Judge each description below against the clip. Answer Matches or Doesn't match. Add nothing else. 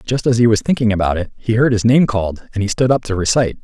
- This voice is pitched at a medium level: Doesn't match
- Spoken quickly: Matches